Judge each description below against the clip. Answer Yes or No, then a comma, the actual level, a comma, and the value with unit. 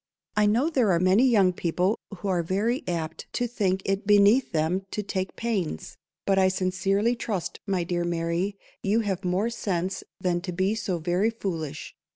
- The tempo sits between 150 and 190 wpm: Yes, average, 185 wpm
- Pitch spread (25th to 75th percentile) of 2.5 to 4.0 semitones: Yes, average, 2.9 semitones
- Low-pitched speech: No, high, 190 Hz